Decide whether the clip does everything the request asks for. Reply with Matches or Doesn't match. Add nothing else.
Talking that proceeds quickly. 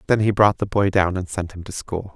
Matches